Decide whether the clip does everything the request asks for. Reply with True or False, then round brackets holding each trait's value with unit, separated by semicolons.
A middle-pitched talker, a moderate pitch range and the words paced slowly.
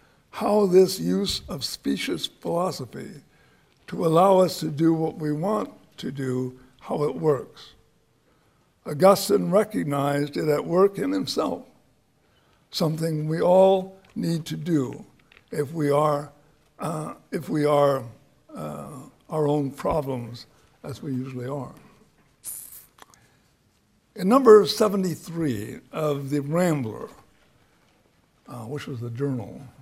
True (150 Hz; 4.3 semitones; 115 wpm)